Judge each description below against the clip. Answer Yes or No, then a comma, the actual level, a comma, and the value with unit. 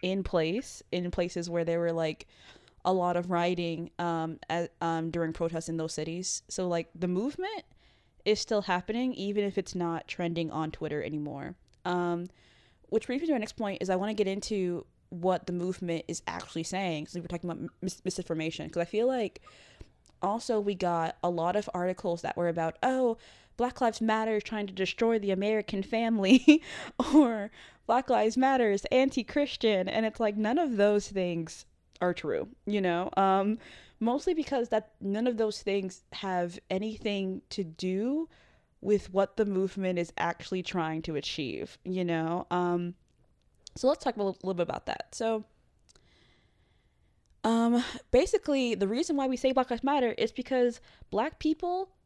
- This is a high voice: Yes, high, 195 Hz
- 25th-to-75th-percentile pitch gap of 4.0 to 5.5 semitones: Yes, average, 4.7 semitones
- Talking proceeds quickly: No, average, 175 wpm